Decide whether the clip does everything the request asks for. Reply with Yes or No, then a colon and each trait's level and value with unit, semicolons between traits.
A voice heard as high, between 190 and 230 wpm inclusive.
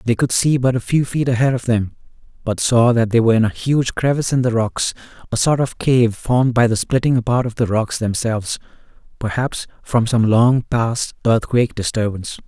No: low, 120 Hz; average, 200 wpm